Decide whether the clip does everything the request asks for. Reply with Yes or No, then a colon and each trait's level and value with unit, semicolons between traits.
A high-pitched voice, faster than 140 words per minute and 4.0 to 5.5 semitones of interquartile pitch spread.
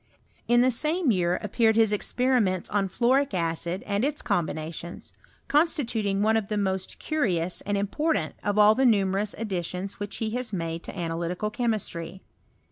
Yes: high, 205 Hz; average, 160 wpm; average, 4.4 semitones